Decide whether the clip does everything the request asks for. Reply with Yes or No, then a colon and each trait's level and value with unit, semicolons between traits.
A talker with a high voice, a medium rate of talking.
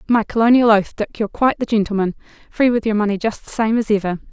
No: high, 215 Hz; fast, 220 wpm